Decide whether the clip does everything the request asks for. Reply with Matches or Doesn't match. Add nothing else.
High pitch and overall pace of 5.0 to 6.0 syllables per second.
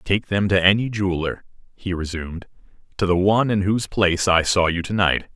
Doesn't match